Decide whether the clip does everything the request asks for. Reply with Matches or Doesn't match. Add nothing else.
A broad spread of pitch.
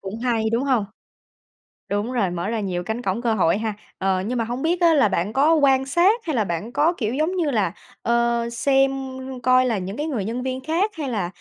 Doesn't match